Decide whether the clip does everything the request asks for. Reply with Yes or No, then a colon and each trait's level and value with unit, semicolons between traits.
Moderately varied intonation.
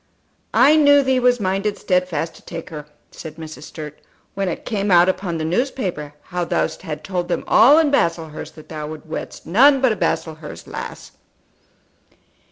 No: wide, 6.8 semitones